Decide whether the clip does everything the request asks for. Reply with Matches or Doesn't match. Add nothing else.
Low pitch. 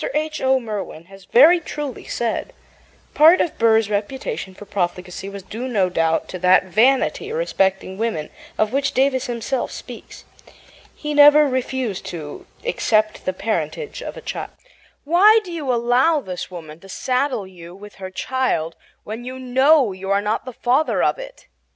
Doesn't match